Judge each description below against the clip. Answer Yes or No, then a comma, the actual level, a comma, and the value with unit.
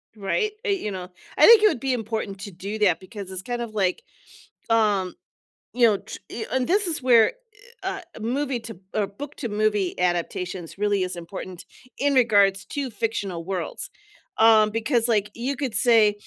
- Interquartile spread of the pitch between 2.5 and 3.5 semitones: No, average, 4.1 semitones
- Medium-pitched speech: No, high, 215 Hz